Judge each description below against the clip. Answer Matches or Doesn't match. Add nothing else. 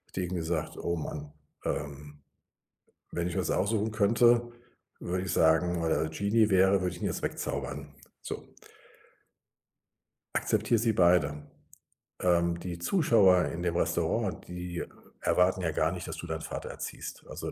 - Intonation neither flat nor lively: Matches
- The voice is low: Matches